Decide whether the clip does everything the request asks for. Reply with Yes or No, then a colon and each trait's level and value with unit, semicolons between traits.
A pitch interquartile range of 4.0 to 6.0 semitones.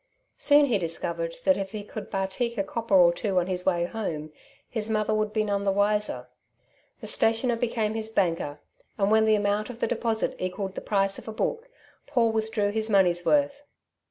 No: average, 2.7 semitones